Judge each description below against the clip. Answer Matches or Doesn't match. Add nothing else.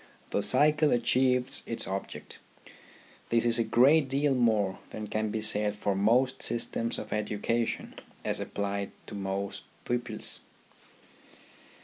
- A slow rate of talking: Matches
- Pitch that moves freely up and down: Doesn't match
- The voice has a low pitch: Matches